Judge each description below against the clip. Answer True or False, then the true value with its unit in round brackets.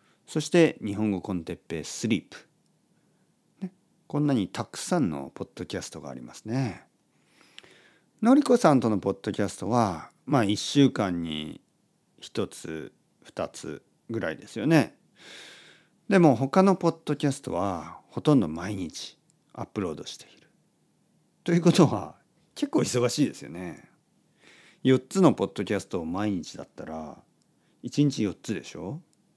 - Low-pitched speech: True (130 Hz)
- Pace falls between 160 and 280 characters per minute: True (270 characters per minute)